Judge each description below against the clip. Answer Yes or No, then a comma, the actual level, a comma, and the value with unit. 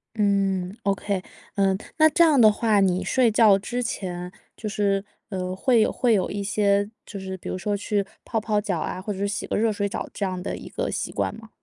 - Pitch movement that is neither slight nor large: No, narrow, 2.1 semitones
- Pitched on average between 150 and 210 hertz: Yes, high, 200 Hz